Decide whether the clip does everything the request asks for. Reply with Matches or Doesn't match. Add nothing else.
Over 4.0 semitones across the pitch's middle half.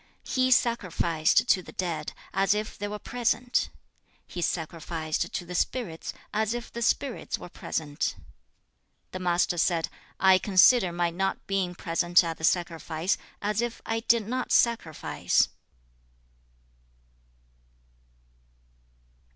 Matches